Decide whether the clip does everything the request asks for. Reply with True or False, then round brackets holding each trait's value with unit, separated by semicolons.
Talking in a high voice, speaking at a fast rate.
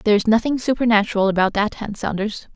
False (215 Hz; 165 wpm)